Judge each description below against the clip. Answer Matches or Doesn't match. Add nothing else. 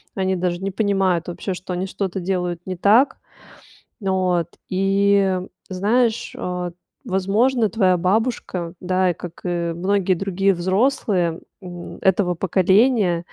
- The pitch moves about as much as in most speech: Doesn't match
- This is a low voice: Doesn't match